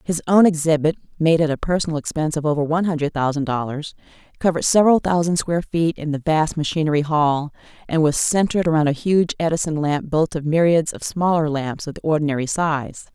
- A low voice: No, medium, 155 Hz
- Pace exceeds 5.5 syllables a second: Yes, 6.0 syllables/s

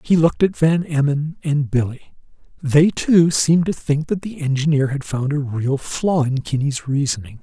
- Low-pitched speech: No, medium, 145 Hz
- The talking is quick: No, average, 185 wpm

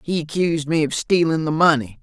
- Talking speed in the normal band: No, fast, 210 wpm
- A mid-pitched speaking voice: Yes, medium, 155 Hz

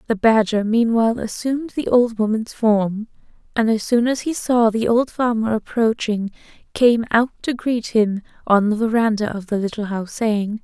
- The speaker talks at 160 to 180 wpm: Yes, average, 175 wpm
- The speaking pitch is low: No, high, 225 Hz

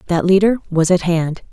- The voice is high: No, medium, 175 Hz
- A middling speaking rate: Yes, average, 195 wpm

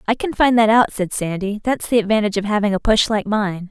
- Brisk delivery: Yes, fast, 260 wpm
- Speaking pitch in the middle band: No, high, 210 Hz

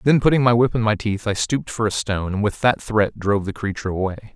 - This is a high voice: No, low, 105 Hz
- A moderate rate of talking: No, fast, 275 wpm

